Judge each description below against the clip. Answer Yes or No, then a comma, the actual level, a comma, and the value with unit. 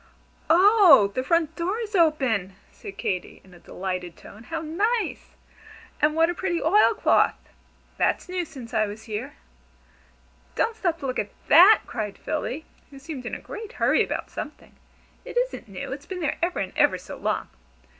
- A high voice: Yes, very high, 310 Hz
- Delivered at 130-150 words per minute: No, average, 175 wpm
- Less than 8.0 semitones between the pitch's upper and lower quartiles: No, wide, 8.7 semitones